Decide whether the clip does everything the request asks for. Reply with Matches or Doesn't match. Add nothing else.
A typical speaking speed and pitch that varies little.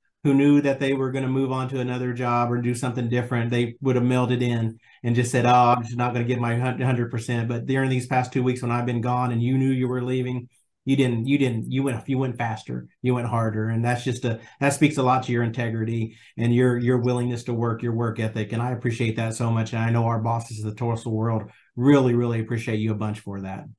Doesn't match